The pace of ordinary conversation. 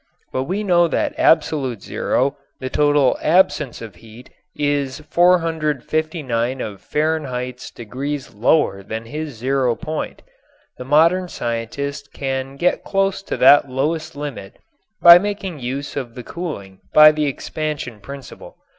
No: slow, 130 wpm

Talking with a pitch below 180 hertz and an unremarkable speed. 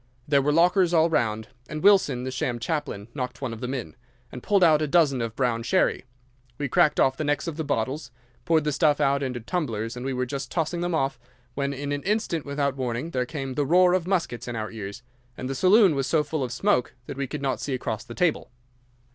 No: medium, 140 Hz; fast, 230 wpm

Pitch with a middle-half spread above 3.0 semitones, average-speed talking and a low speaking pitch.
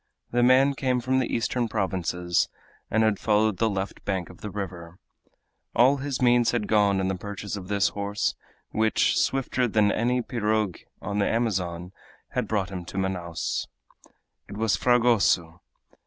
Yes: average, 4.1 semitones; average, 165 wpm; low, 105 Hz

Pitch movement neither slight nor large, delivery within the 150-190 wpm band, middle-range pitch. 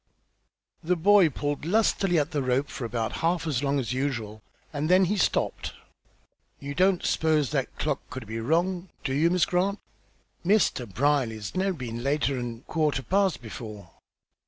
No: wide, 6.3 semitones; average, 160 wpm; medium, 145 Hz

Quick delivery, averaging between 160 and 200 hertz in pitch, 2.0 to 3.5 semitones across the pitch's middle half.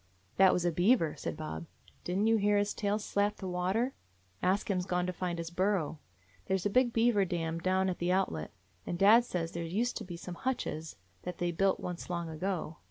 Yes: fast, 220 wpm; medium, 185 Hz; average, 2.9 semitones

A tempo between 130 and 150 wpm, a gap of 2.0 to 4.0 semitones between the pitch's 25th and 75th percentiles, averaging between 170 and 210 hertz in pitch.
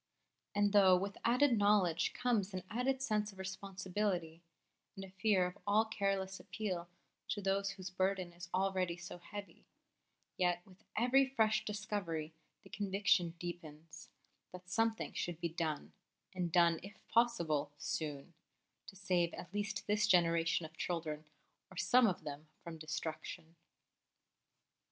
Yes: average, 140 wpm; average, 3.3 semitones; medium, 185 Hz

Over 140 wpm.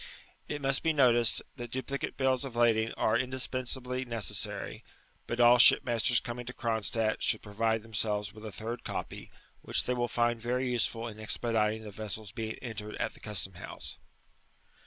Yes: average, 165 wpm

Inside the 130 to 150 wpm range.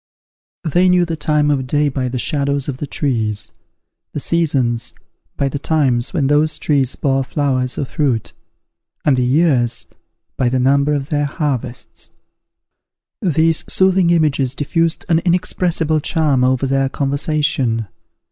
Yes: average, 140 wpm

